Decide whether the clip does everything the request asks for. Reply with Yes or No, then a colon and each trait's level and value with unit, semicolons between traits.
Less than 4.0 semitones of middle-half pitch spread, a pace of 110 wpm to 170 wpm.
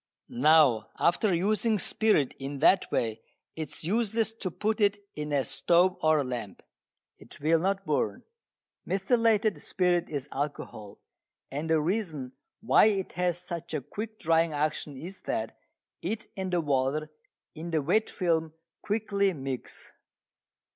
No: average, 5.1 semitones; average, 145 wpm